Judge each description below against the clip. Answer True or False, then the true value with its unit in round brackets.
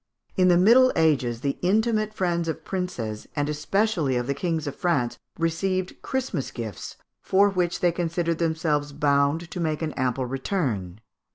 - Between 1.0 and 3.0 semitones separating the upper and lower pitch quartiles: False (4.6 semitones)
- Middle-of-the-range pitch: True (165 Hz)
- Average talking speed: True (160 wpm)